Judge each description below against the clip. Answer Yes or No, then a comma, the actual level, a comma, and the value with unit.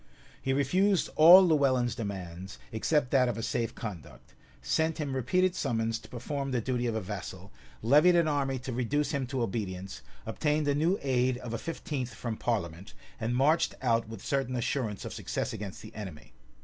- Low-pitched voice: Yes, low, 125 Hz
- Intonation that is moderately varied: Yes, average, 4.5 semitones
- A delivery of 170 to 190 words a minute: Yes, average, 180 wpm